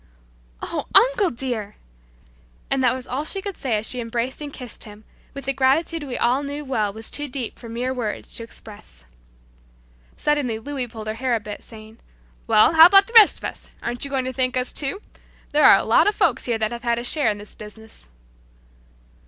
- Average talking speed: No, fast, 210 wpm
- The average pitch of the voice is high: Yes, very high, 250 Hz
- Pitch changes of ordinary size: Yes, average, 4.2 semitones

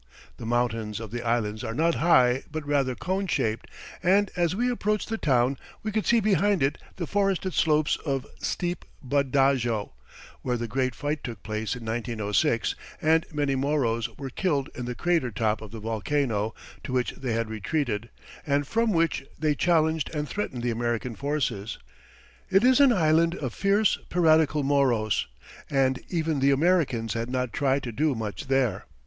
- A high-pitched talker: No, low, 135 Hz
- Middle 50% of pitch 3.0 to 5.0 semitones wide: No, wide, 5.6 semitones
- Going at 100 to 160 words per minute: No, average, 175 wpm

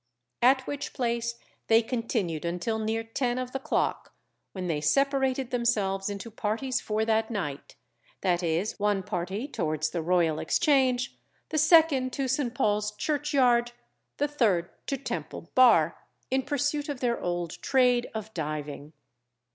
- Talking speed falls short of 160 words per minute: Yes, average, 140 wpm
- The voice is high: Yes, high, 230 Hz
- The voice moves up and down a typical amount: No, wide, 5.9 semitones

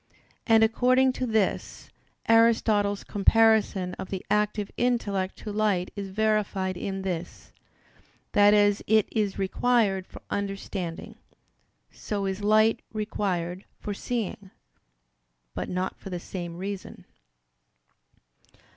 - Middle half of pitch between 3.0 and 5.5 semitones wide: No, narrow, 2.4 semitones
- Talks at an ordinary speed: No, slow, 110 wpm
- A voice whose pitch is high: Yes, high, 205 Hz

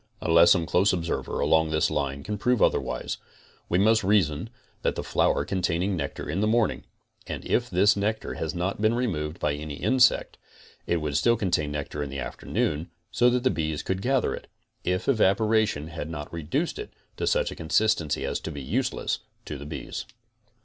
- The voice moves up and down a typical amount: No, wide, 5.7 semitones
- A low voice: Yes, very low, 85 Hz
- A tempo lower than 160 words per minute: No, average, 185 wpm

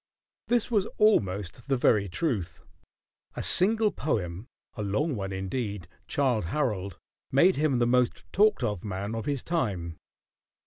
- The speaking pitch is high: No, low, 115 Hz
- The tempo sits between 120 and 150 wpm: Yes, average, 140 wpm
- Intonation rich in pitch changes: Yes, wide, 7.7 semitones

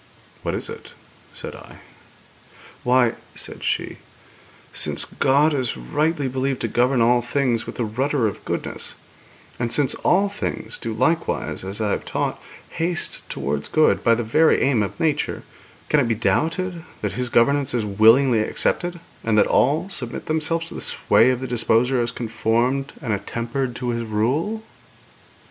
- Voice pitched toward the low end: Yes, low, 125 Hz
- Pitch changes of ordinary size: Yes, average, 4.2 semitones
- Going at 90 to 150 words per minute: No, average, 160 wpm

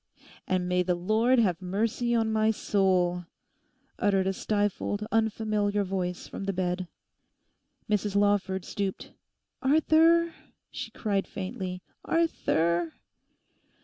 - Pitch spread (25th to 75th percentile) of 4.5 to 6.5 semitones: No, average, 3.2 semitones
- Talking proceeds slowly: Yes, slow, 110 wpm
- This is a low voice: No, high, 200 Hz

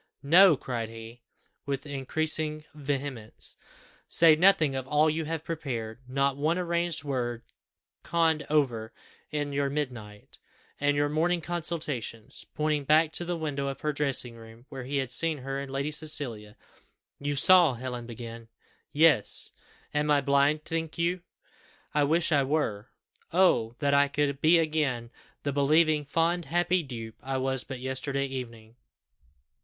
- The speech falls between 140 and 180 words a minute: Yes, average, 150 wpm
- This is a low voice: No, medium, 145 Hz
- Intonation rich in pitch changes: No, average, 3.5 semitones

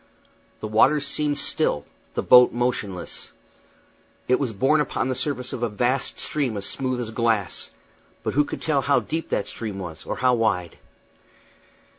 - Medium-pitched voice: No, low, 125 Hz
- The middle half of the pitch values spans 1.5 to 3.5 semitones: No, average, 4.3 semitones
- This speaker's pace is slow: No, average, 165 wpm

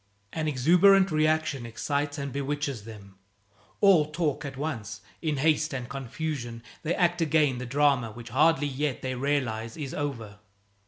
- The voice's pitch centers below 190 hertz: Yes, medium, 140 Hz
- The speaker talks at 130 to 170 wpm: Yes, average, 150 wpm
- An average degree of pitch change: Yes, average, 3.9 semitones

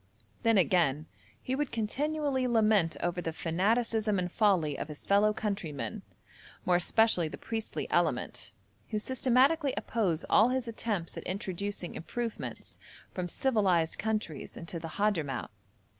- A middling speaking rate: No, slow, 130 wpm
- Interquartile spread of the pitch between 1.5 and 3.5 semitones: No, average, 4.9 semitones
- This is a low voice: No, high, 210 Hz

